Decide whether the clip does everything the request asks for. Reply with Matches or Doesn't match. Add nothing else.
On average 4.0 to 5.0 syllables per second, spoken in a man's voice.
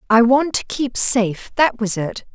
Doesn't match